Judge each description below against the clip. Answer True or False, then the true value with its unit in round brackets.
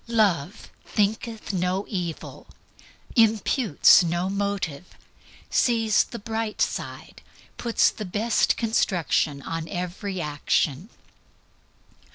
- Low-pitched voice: False (200 Hz)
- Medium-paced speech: False (90 wpm)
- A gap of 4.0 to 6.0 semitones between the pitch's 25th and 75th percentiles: True (4.3 semitones)